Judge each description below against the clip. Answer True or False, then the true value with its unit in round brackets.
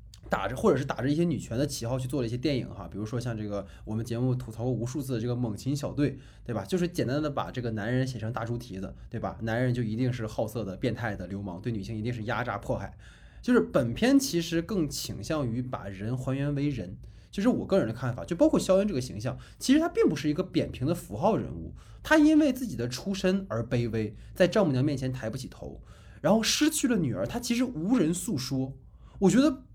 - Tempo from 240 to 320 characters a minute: False (355 characters per minute)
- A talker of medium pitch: False (130 Hz)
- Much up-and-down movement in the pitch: True (7.2 semitones)